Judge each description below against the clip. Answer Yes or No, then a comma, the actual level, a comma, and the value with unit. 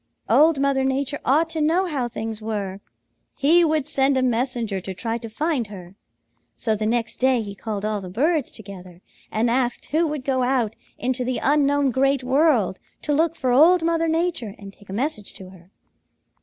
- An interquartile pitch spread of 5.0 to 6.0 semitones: Yes, average, 5.3 semitones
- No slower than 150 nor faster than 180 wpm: No, average, 190 wpm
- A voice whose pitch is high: Yes, very high, 255 Hz